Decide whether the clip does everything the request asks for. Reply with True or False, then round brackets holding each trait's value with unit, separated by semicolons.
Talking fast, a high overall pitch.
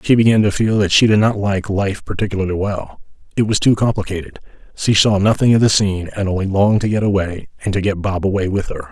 False (235 wpm; 100 Hz)